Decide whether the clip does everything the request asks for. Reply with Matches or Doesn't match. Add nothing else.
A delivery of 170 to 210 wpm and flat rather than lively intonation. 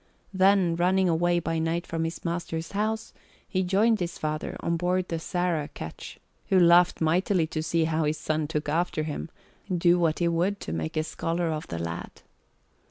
Matches